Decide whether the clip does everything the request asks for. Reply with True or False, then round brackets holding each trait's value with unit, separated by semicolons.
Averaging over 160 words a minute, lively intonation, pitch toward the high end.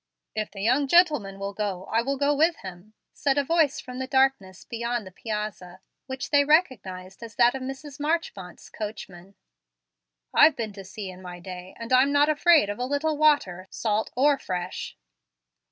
True (180 wpm; 6.5 semitones; 235 Hz)